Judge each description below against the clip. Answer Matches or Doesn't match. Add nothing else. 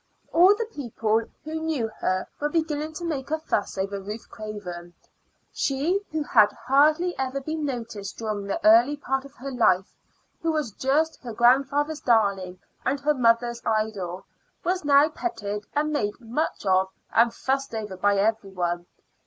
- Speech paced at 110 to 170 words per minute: Matches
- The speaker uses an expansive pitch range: Matches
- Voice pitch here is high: Matches